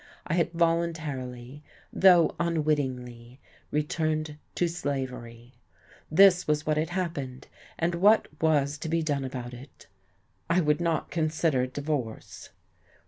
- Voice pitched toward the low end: No, medium, 150 Hz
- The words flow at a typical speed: No, slow, 120 wpm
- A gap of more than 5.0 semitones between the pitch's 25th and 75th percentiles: No, average, 4.2 semitones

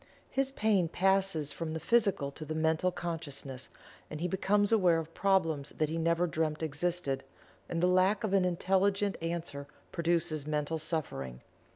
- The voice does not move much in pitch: No, average, 3.4 semitones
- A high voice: No, medium, 170 Hz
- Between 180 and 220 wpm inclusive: No, average, 160 wpm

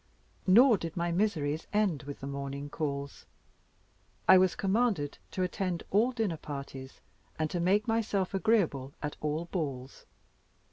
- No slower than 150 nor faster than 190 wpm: No, average, 140 wpm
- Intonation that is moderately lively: No, wide, 5.7 semitones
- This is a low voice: No, medium, 170 Hz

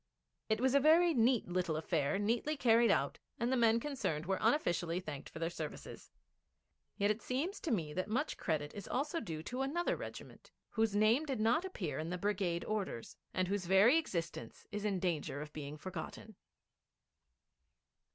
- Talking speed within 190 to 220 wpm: No, average, 175 wpm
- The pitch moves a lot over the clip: Yes, wide, 6.5 semitones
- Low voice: No, high, 205 Hz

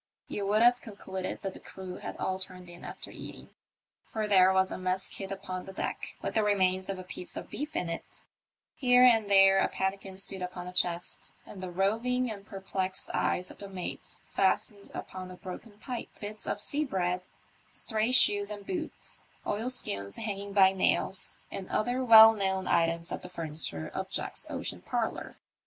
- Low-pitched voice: No, high, 195 Hz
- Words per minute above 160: Yes, average, 185 wpm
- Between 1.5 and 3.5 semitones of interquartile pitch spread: Yes, narrow, 2.6 semitones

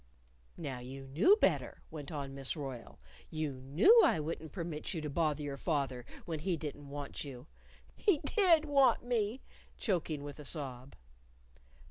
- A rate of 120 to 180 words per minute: Yes, average, 160 wpm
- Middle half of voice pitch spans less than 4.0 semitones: No, average, 4.3 semitones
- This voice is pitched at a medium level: Yes, medium, 150 Hz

